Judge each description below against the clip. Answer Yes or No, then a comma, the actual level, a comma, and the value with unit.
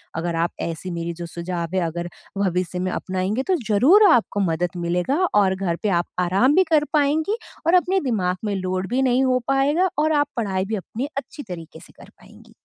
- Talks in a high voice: Yes, high, 195 Hz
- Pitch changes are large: Yes, wide, 7.3 semitones